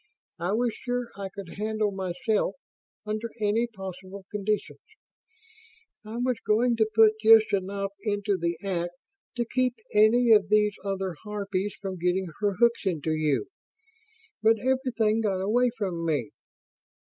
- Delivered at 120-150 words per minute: Yes, average, 140 wpm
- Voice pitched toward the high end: Yes, high, 210 Hz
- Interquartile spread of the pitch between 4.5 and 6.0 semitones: No, average, 2.8 semitones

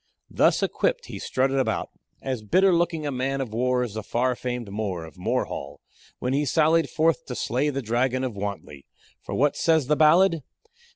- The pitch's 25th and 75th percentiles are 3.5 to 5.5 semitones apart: Yes, average, 4.5 semitones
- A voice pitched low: Yes, low, 130 Hz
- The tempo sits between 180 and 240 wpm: Yes, average, 185 wpm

